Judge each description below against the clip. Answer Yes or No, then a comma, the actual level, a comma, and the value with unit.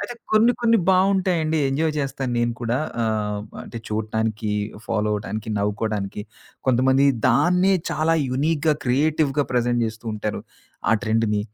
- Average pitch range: No, wide, 6.3 semitones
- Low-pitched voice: Yes, low, 125 Hz